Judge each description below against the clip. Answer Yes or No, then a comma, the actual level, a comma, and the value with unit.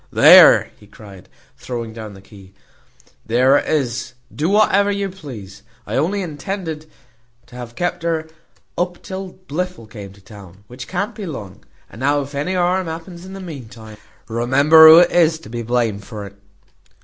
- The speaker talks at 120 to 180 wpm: Yes, average, 175 wpm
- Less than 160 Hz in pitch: Yes, medium, 140 Hz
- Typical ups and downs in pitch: No, wide, 7.9 semitones